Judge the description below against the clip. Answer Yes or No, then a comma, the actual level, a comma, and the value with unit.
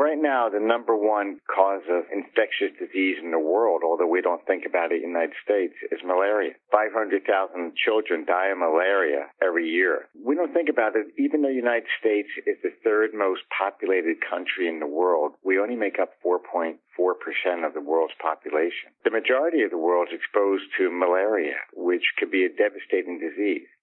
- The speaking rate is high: No, average, 185 wpm